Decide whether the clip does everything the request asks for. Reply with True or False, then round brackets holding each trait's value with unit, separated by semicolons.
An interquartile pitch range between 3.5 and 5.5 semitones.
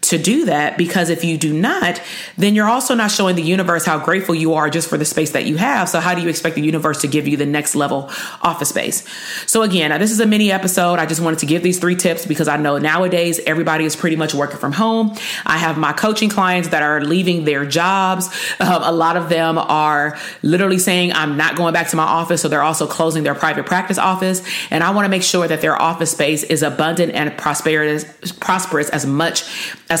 False (2.9 semitones)